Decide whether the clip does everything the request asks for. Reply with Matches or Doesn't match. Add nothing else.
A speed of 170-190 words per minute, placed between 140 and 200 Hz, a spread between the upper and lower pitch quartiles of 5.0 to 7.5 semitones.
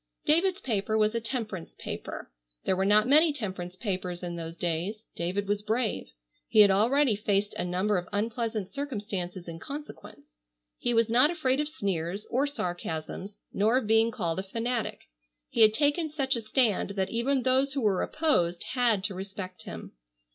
Doesn't match